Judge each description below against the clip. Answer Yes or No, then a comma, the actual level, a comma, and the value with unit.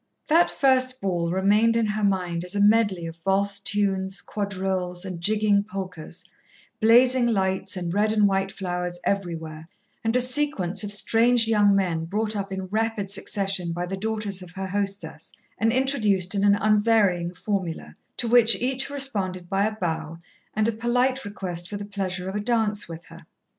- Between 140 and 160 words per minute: No, average, 175 wpm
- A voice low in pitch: No, high, 200 Hz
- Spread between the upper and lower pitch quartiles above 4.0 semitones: No, average, 3.2 semitones